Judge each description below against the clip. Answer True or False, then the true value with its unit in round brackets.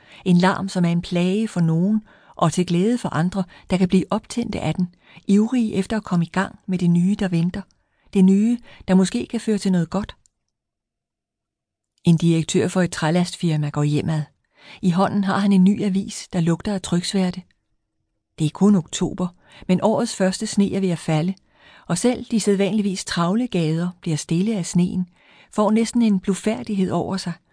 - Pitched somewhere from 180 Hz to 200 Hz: True (185 Hz)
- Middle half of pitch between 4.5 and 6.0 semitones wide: False (2.8 semitones)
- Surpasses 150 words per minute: True (185 wpm)